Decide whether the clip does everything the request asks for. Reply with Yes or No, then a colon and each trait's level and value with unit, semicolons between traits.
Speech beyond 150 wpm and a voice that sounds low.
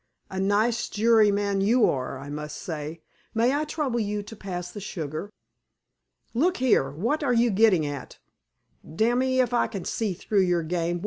No: average, 170 wpm; high, 205 Hz